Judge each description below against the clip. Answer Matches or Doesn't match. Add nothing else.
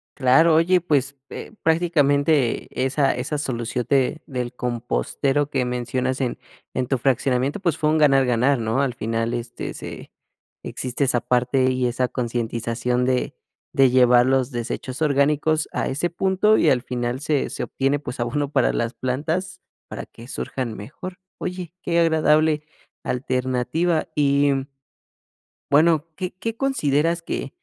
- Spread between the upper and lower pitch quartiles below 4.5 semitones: Matches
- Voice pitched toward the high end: Doesn't match